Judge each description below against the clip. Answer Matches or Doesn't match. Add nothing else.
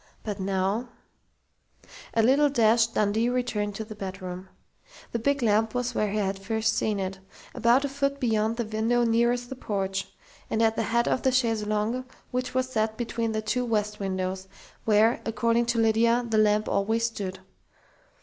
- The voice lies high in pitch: Matches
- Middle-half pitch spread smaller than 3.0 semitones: Matches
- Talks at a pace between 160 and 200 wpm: Matches